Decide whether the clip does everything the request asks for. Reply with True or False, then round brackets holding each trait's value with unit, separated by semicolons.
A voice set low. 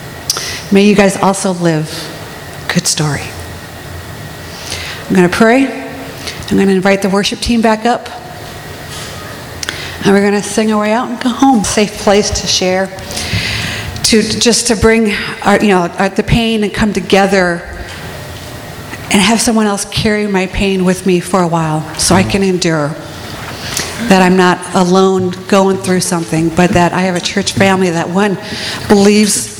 False (195 Hz)